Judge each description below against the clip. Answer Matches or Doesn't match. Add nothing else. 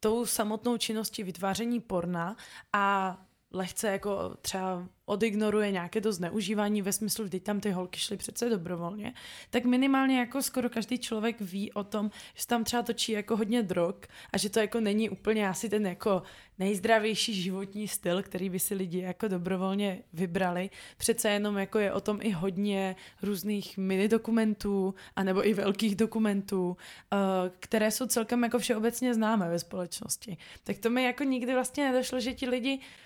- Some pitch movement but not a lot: Matches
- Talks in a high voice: Matches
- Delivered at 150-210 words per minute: Matches